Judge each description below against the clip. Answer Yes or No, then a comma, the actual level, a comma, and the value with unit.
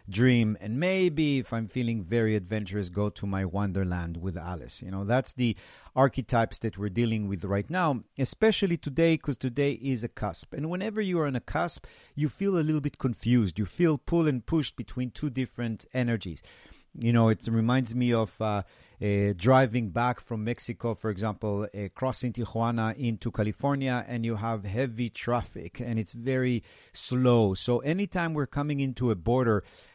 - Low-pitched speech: Yes, low, 120 Hz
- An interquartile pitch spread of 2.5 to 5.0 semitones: Yes, average, 3.9 semitones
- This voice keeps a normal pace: Yes, average, 180 wpm